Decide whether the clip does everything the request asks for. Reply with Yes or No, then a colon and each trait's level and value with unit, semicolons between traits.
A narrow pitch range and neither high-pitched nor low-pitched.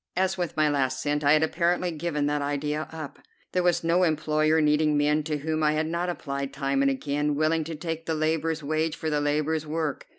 Yes: narrow, 1.7 semitones; medium, 155 Hz